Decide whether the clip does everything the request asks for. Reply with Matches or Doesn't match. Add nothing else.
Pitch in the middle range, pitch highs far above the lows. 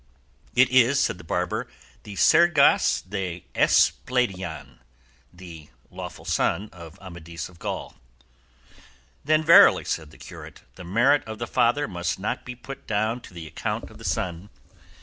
Doesn't match